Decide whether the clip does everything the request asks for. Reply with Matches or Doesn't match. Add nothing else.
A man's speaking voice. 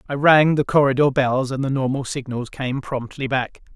Matches